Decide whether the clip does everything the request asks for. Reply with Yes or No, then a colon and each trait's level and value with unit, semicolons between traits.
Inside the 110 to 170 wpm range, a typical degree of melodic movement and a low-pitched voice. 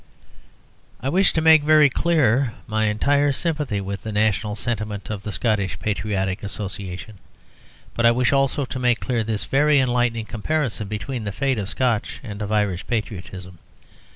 Yes: average, 160 wpm; average, 4.5 semitones; low, 110 Hz